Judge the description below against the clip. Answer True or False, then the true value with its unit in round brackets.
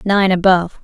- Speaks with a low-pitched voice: False (185 Hz)